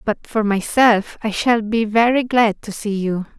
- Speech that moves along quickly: No, average, 195 wpm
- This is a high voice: Yes, high, 220 Hz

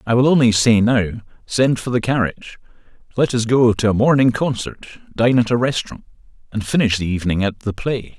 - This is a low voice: Yes, low, 115 Hz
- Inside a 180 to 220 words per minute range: Yes, average, 200 wpm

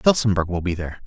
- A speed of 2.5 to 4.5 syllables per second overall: No, 6.9 syllables/s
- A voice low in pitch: Yes, very low, 95 Hz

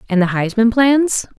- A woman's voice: Yes, female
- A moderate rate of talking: Yes, average, 175 wpm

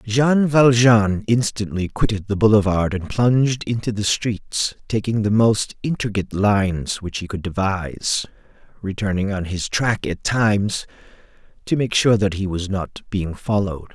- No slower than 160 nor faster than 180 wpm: No, average, 150 wpm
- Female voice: No, male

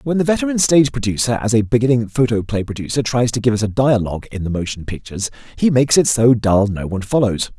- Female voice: No, male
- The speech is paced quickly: Yes, fast, 220 wpm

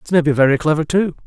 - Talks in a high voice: No, medium, 155 Hz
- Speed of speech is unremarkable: No, fast, 285 wpm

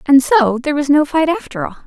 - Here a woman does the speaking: Yes, female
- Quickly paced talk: Yes, fast, 255 wpm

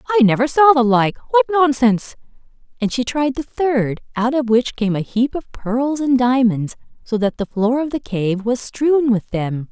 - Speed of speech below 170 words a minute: No, average, 200 wpm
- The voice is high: Yes, very high, 250 Hz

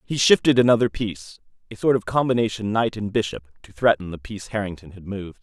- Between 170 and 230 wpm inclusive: Yes, average, 200 wpm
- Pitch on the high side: No, low, 105 Hz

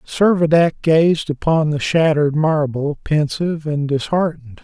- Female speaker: No, male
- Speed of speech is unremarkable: No, slow, 115 wpm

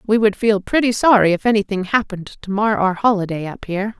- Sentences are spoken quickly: Yes, fast, 210 wpm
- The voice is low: No, high, 205 Hz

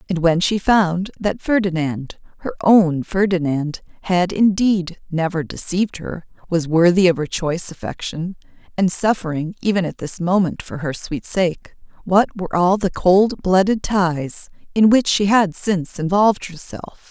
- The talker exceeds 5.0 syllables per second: No, 4.4 syllables/s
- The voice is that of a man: No, female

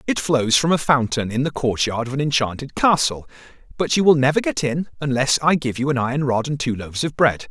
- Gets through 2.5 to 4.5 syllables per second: No, 5.8 syllables/s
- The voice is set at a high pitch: No, low, 135 Hz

